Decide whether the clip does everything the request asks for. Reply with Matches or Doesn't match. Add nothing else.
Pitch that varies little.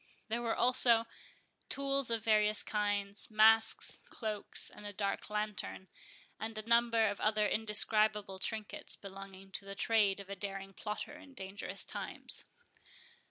Matches